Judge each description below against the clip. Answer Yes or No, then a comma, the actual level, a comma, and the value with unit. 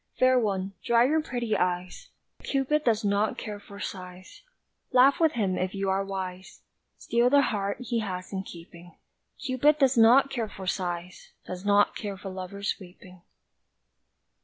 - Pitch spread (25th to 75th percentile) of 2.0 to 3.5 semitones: No, average, 4.9 semitones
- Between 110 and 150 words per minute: No, average, 160 wpm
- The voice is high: Yes, high, 200 Hz